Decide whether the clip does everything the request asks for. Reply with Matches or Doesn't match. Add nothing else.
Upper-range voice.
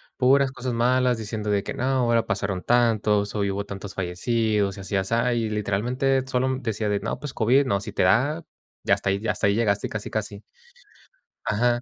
Doesn't match